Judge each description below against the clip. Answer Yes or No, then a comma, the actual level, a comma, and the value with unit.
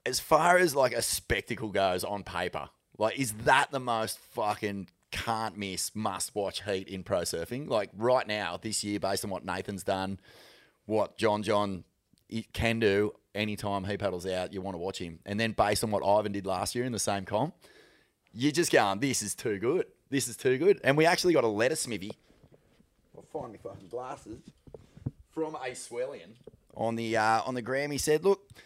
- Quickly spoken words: No, average, 195 wpm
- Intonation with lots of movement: No, average, 4.2 semitones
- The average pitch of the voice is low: Yes, low, 105 Hz